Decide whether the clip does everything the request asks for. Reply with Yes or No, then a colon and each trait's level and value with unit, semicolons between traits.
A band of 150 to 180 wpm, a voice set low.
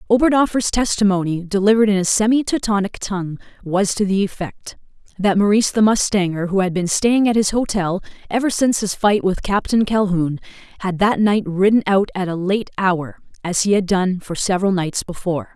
No: average, 175 wpm; high, 200 Hz